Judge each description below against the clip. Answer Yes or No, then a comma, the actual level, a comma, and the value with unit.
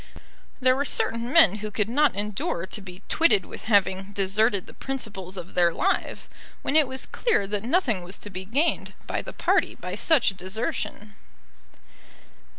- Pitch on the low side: No, high, 210 Hz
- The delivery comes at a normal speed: Yes, average, 165 wpm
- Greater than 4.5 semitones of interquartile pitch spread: Yes, average, 5.2 semitones